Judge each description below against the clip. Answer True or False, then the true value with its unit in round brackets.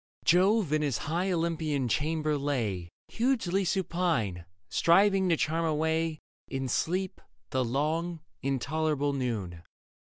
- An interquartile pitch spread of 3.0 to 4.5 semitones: True (4.2 semitones)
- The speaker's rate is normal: False (110 wpm)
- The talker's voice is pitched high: False (155 Hz)